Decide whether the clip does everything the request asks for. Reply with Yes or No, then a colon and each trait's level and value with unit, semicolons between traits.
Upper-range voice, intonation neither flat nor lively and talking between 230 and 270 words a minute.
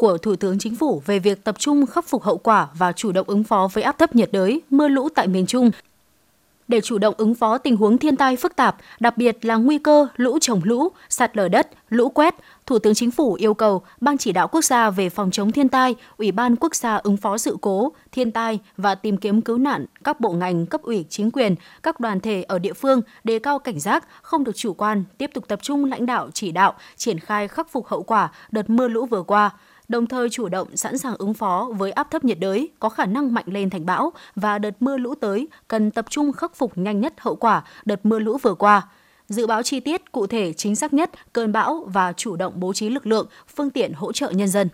Yes: high, 225 Hz; average, 4.4 semitones; fast, 250 wpm